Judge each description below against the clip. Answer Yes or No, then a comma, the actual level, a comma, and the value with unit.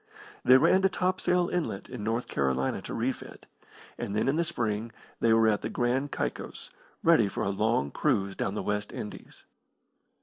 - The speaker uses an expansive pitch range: Yes, wide, 6.0 semitones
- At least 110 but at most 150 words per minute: No, average, 175 wpm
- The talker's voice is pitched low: Yes, low, 115 Hz